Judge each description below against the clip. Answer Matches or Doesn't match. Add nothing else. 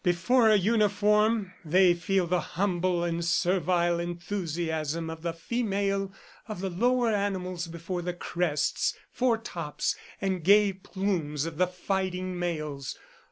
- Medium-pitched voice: Matches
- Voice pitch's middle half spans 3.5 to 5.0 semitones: Doesn't match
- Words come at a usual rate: Doesn't match